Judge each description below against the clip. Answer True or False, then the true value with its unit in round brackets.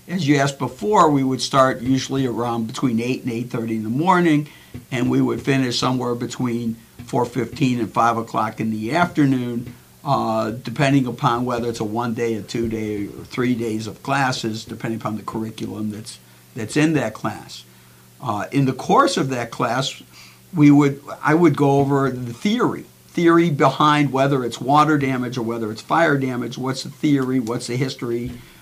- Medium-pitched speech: False (125 Hz)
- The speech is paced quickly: False (185 wpm)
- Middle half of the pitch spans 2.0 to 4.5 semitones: True (3.4 semitones)